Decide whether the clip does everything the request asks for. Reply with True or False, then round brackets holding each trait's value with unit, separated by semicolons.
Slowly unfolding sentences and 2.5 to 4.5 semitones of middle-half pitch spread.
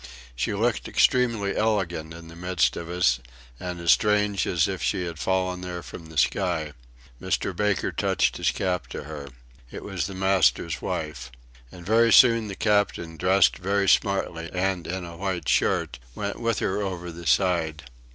False (170 wpm; 3.0 semitones)